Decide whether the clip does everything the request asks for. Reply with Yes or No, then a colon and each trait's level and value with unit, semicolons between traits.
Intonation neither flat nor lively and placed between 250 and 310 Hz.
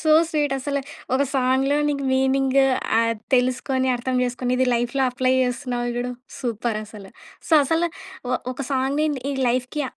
No: narrow, 1.9 semitones; very high, 260 Hz